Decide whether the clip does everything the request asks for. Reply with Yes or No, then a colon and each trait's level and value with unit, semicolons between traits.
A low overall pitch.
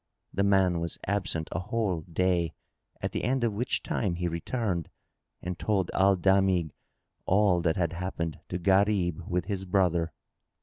Yes: very low, 90 Hz